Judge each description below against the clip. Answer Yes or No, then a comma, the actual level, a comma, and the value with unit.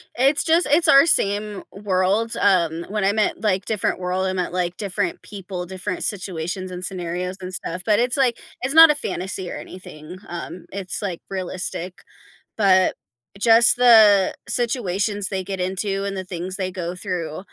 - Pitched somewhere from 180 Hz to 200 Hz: Yes, high, 190 Hz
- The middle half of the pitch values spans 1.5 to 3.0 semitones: Yes, narrow, 2.6 semitones